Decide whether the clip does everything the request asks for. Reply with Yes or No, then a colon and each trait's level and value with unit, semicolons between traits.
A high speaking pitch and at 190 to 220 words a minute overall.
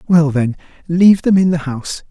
No: medium, 165 Hz; average, 200 wpm